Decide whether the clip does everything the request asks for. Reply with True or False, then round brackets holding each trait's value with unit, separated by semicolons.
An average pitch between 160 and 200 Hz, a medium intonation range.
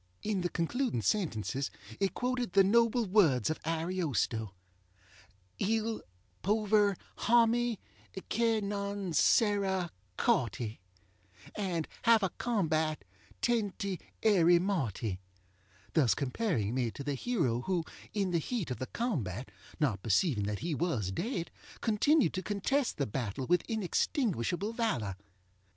False (185 Hz; 8.1 semitones)